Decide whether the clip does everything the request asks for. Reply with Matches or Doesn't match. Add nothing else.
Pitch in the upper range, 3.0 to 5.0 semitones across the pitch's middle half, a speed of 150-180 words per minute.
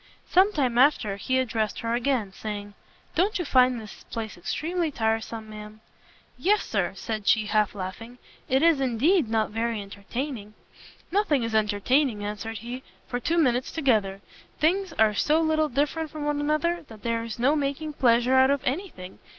Doesn't match